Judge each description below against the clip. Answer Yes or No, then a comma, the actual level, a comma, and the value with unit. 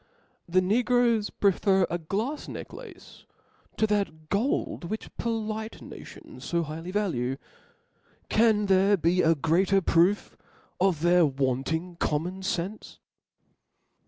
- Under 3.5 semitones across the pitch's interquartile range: No, average, 4.1 semitones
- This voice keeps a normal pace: No, slow, 110 wpm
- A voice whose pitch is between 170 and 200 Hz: Yes, medium, 185 Hz